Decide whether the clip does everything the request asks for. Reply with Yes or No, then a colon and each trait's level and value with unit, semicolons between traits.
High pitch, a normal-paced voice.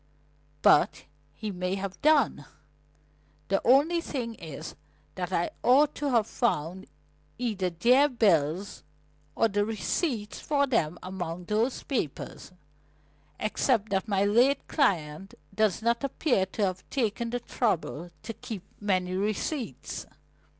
No: high, 210 Hz; slow, 125 wpm